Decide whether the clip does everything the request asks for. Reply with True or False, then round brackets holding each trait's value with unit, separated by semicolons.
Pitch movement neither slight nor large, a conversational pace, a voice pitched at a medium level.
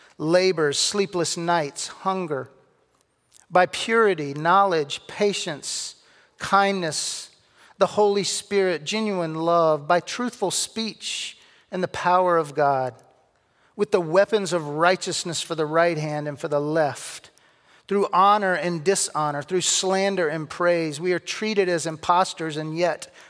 False (3.5 semitones; 130 wpm; 175 Hz)